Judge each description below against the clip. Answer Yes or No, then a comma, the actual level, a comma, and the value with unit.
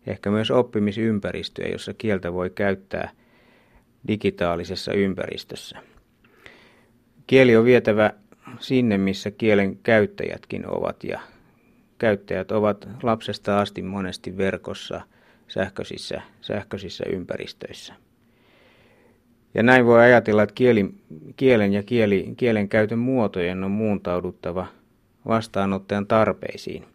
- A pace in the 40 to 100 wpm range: Yes, slow, 95 wpm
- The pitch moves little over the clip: No, average, 3.2 semitones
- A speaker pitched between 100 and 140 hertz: Yes, low, 105 Hz